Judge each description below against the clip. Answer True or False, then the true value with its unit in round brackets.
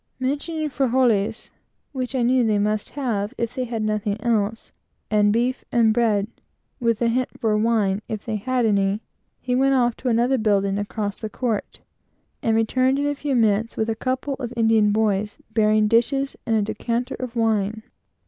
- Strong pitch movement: False (3.0 semitones)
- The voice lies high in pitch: True (225 Hz)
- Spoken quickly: False (175 wpm)